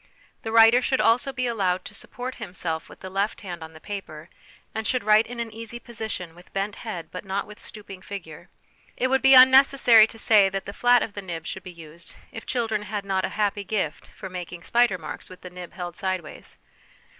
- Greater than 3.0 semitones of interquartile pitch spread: Yes, average, 4.0 semitones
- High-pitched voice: Yes, high, 205 Hz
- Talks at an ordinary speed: No, fast, 215 wpm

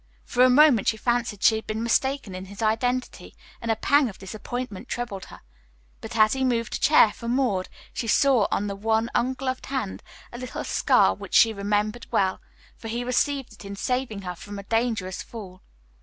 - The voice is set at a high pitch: Yes, high, 225 Hz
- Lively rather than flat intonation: No, average, 3.5 semitones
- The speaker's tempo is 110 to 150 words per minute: No, average, 195 wpm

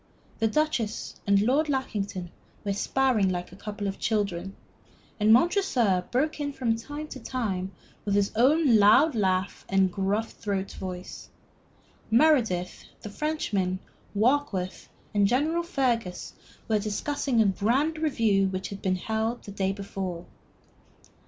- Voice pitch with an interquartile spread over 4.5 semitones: Yes, average, 5.3 semitones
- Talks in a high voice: Yes, high, 215 Hz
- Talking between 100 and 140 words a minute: Yes, slow, 135 wpm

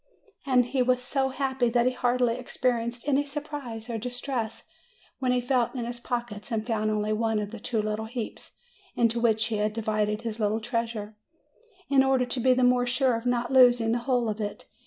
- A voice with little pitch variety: Yes, narrow, 2.2 semitones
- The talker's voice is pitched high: Yes, high, 240 Hz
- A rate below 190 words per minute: No, average, 200 wpm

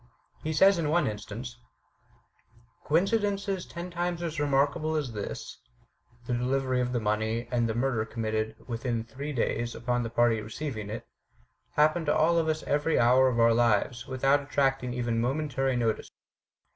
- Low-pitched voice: Yes, low, 130 Hz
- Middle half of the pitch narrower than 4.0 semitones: No, average, 4.7 semitones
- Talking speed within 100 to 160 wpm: Yes, average, 155 wpm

